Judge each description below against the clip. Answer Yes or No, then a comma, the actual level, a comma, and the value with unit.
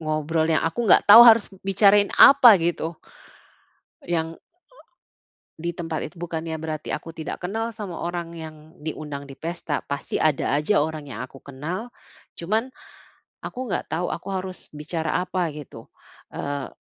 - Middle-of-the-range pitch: Yes, medium, 165 Hz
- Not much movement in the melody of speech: No, average, 3.1 semitones